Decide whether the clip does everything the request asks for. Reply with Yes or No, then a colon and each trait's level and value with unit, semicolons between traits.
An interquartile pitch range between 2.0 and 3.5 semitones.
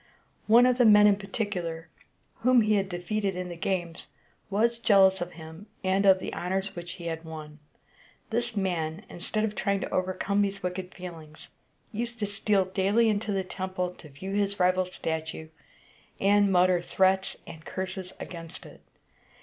Yes: narrow, 2.6 semitones